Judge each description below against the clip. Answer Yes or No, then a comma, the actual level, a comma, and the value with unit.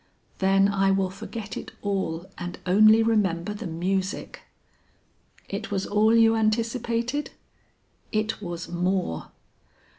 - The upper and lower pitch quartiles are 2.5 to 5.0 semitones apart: Yes, average, 2.9 semitones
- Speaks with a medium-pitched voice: No, high, 200 Hz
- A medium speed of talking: No, slow, 115 wpm